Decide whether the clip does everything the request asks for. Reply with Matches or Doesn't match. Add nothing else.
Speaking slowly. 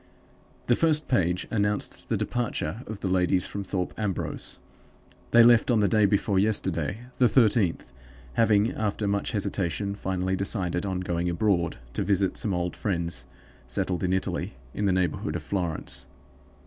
Doesn't match